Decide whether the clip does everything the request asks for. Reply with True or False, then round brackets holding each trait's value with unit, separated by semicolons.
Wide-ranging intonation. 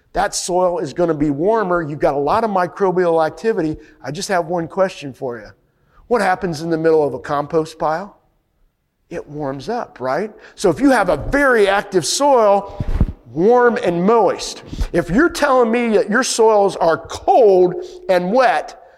True (6.0 semitones)